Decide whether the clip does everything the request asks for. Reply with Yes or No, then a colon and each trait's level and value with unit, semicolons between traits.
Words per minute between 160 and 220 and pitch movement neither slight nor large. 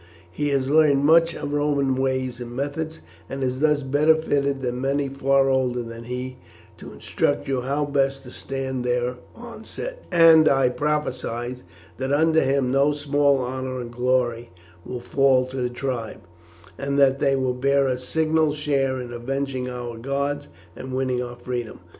No: average, 165 wpm; narrow, 2.2 semitones